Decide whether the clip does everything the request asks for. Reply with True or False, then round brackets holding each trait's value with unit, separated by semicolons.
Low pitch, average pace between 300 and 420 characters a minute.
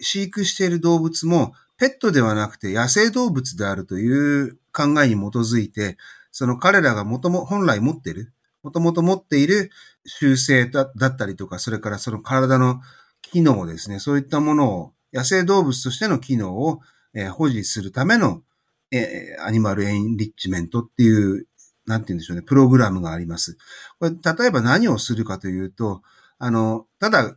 True (130 Hz; 345 characters per minute)